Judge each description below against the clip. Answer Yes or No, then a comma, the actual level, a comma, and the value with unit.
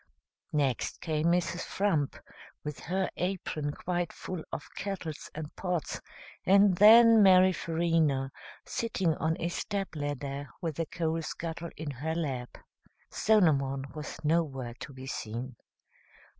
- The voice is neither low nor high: Yes, medium, 160 Hz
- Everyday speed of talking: No, slow, 130 wpm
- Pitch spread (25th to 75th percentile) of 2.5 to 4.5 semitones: Yes, average, 3.9 semitones